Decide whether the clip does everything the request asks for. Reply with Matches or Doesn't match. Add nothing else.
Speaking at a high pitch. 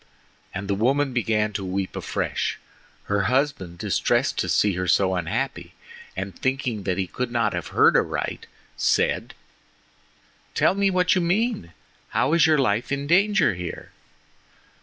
Doesn't match